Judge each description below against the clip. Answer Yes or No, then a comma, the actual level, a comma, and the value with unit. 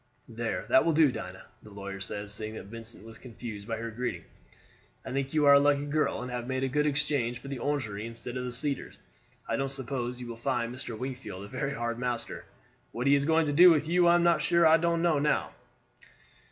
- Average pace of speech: No, fast, 225 wpm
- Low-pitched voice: Yes, low, 130 Hz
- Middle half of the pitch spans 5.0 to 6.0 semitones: No, average, 4.1 semitones